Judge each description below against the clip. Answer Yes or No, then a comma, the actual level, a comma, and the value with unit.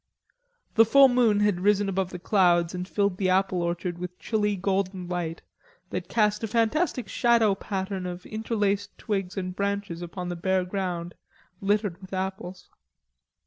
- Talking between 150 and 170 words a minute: Yes, average, 155 wpm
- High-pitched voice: Yes, high, 195 Hz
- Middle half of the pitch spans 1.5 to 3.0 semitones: Yes, narrow, 2.5 semitones